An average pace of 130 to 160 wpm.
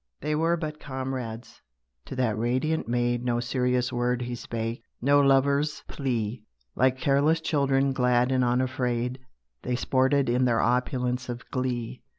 Yes: average, 145 wpm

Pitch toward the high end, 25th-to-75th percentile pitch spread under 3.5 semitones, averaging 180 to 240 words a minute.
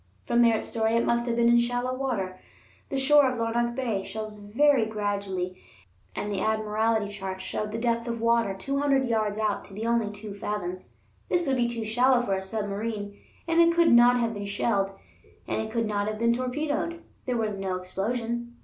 Yes: high, 225 Hz; average, 2.9 semitones; average, 200 wpm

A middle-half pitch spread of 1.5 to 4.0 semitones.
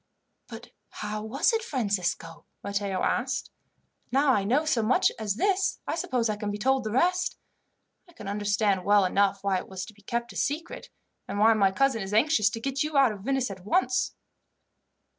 No: average, 4.8 semitones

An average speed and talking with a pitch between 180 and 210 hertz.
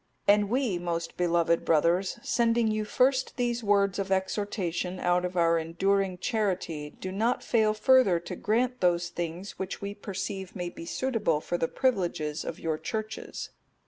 Yes: average, 165 wpm; high, 190 Hz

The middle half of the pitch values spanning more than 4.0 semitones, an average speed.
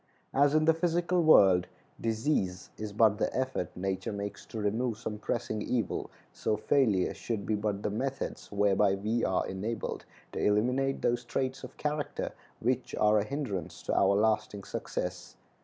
Yes: average, 4.5 semitones; average, 160 wpm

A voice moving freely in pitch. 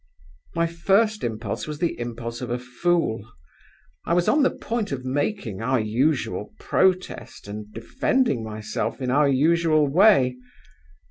Yes: wide, 6.8 semitones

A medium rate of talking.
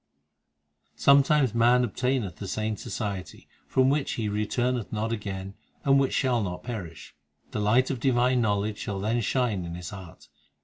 Yes: average, 165 wpm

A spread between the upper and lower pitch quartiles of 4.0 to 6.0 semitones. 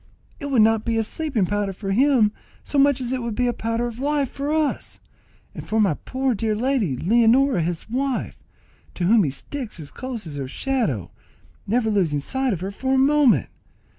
Yes: average, 5.0 semitones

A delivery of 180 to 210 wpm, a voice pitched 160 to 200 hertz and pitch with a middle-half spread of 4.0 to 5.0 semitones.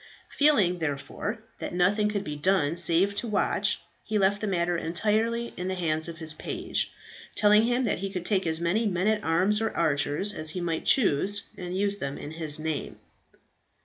Yes: average, 190 wpm; medium, 185 Hz; average, 4.3 semitones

